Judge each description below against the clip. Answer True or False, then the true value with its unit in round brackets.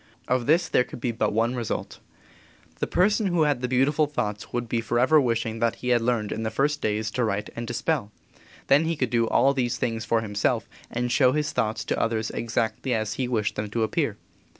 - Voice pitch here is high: False (120 Hz)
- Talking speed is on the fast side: True (220 wpm)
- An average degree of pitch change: True (3.1 semitones)